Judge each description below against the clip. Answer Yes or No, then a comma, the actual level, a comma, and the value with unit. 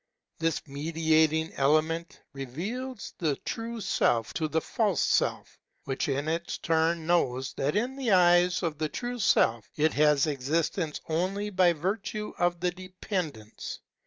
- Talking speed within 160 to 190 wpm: No, average, 140 wpm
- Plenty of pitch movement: No, average, 3.8 semitones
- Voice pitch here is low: No, medium, 165 Hz